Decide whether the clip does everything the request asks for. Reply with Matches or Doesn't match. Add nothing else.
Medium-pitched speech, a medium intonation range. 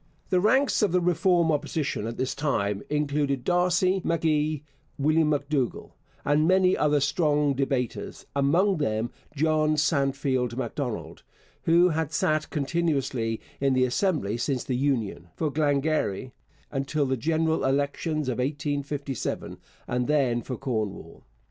Matches